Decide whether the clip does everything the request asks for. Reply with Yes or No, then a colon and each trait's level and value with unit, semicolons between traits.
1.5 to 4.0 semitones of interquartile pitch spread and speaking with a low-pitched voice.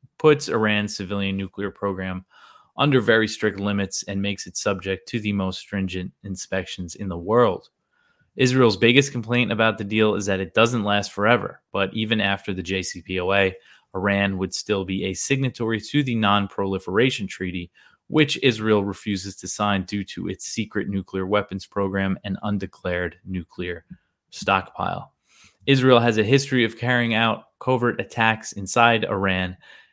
Yes: average, 3.0 semitones; low, 100 Hz